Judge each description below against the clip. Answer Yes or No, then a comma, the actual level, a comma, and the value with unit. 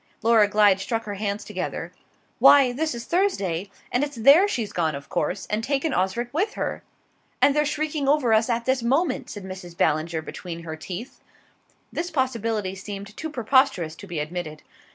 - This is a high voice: Yes, high, 225 Hz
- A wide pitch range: Yes, wide, 6.7 semitones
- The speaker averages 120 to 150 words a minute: No, average, 175 wpm